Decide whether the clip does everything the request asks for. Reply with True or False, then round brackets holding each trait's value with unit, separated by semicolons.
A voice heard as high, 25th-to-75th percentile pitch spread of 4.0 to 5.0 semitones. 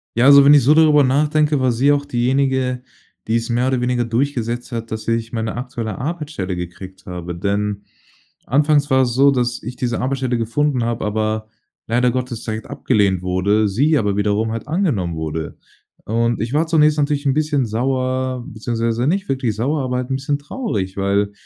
False (125 Hz; 4.3 semitones)